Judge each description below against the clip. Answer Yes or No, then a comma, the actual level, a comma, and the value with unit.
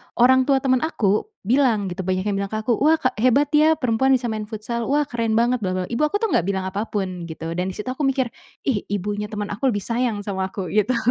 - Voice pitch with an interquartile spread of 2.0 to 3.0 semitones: No, average, 4.6 semitones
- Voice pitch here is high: Yes, high, 225 Hz